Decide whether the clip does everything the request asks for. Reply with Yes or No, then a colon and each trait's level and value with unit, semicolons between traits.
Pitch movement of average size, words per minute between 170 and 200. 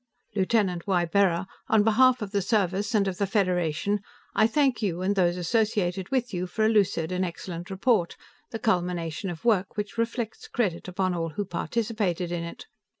Yes: average, 3.6 semitones; average, 175 wpm